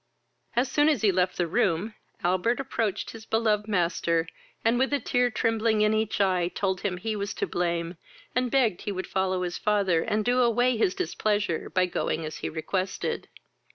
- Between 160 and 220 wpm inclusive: Yes, average, 190 wpm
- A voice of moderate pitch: No, high, 205 Hz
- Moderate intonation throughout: Yes, average, 4.0 semitones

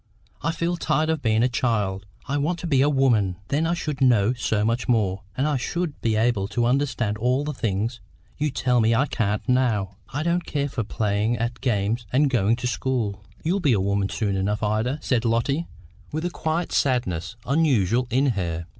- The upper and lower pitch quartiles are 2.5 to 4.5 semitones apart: No, average, 5.1 semitones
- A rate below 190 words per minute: No, average, 200 wpm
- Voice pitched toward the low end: Yes, low, 120 Hz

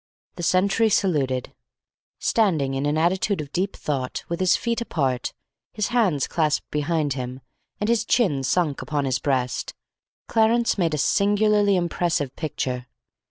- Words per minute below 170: Yes, average, 145 wpm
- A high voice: No, medium, 165 Hz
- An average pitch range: No, wide, 6.5 semitones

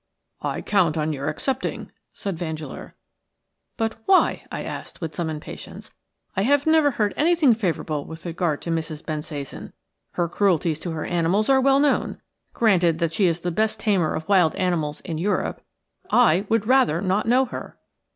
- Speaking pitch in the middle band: Yes, medium, 180 Hz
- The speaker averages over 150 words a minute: Yes, average, 165 wpm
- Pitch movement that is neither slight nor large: No, wide, 5.7 semitones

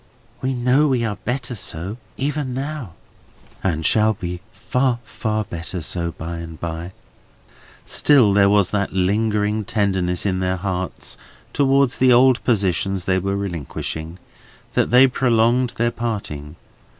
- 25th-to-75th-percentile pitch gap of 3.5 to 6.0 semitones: Yes, average, 5.3 semitones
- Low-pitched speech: Yes, low, 105 Hz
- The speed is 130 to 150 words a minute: Yes, average, 140 wpm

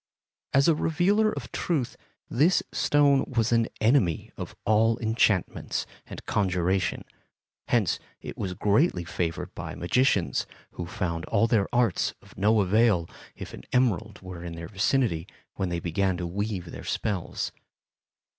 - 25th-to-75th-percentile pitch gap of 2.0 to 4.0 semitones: No, average, 5.3 semitones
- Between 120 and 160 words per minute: Yes, average, 145 wpm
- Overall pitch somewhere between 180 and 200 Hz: No, low, 105 Hz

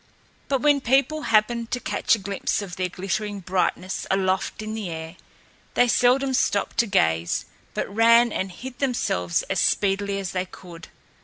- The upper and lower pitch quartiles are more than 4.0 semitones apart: Yes, average, 4.4 semitones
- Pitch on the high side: Yes, high, 200 Hz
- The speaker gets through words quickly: No, average, 165 wpm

